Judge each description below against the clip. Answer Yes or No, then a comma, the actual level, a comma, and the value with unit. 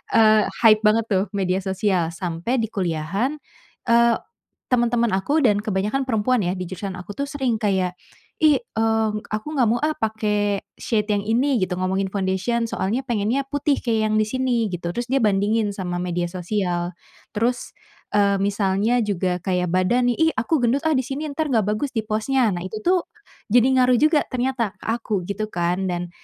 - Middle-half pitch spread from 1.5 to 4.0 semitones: No, average, 4.4 semitones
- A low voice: No, high, 215 Hz